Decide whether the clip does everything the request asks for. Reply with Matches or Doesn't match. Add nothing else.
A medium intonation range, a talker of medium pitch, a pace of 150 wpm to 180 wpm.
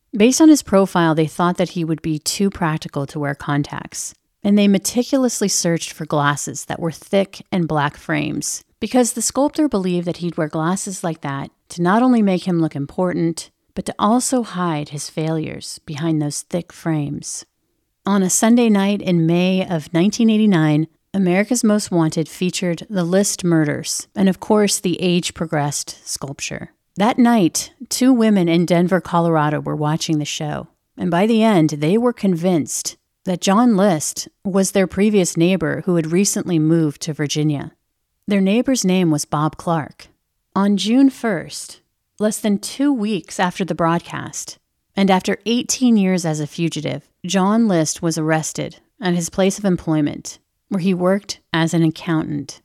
Matches